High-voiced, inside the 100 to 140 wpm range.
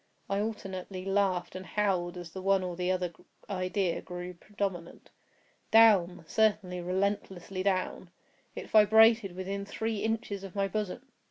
Yes: high, 195 Hz; slow, 135 wpm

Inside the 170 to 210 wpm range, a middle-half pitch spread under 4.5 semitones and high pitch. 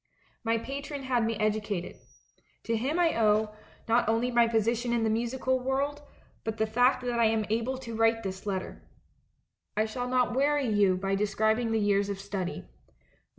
Yes: average, 175 wpm; average, 2.7 semitones; high, 225 Hz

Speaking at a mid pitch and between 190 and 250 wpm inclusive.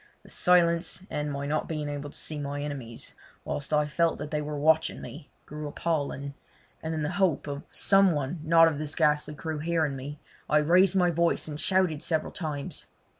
Yes: medium, 150 Hz; average, 195 wpm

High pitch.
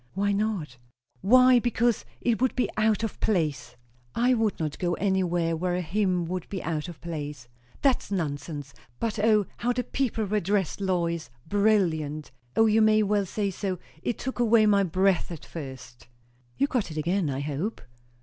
Yes: high, 195 Hz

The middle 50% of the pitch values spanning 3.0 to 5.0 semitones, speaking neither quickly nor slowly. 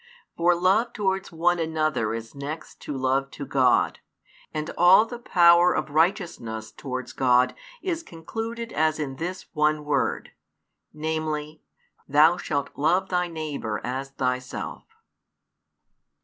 No: average, 4.5 semitones; slow, 125 wpm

